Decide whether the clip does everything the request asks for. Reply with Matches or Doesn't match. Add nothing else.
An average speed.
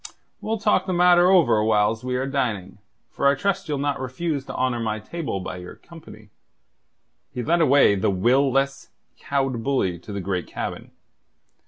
Matches